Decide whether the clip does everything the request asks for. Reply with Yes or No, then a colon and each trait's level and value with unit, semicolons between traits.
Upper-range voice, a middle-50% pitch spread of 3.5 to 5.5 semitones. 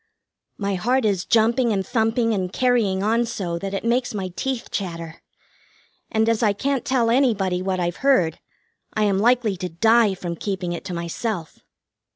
Yes: high, 205 Hz; average, 4.2 semitones